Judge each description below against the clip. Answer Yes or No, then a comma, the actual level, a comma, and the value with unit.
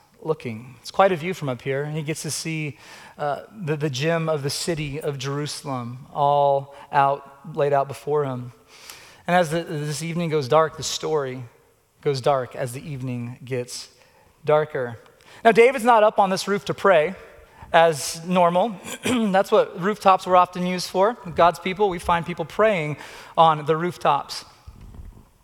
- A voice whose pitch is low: No, medium, 160 Hz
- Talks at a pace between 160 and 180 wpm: Yes, average, 170 wpm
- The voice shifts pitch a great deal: No, average, 4.4 semitones